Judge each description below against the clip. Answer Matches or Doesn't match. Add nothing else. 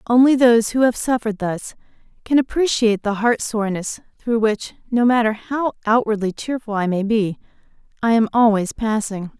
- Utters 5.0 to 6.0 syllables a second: Matches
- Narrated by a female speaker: Matches